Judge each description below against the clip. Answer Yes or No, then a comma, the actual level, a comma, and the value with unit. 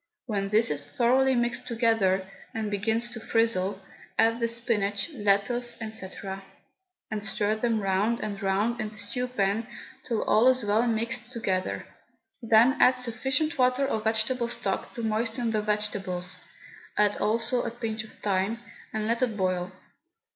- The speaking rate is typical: Yes, average, 155 wpm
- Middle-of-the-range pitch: No, high, 220 Hz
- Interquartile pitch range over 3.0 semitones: No, average, 2.7 semitones